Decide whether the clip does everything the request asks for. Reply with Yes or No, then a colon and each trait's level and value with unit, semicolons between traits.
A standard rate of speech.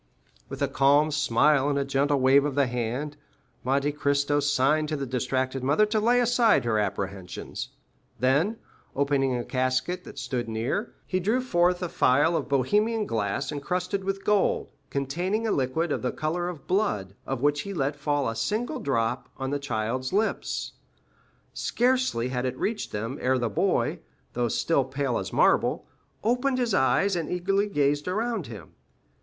Yes: average, 170 wpm